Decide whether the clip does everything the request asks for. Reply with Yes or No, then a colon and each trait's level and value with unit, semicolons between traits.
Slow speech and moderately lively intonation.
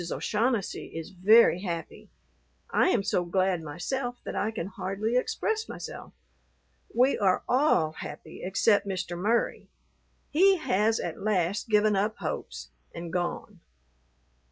Yes: slow, 130 wpm; average, 4.5 semitones